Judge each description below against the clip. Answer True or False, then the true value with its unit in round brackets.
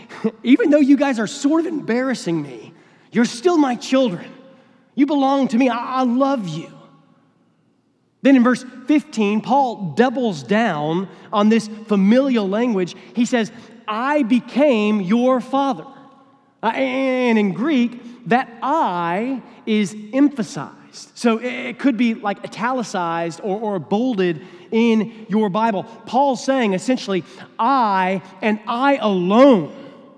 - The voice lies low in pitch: False (235 Hz)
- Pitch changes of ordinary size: True (4.1 semitones)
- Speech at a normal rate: False (125 wpm)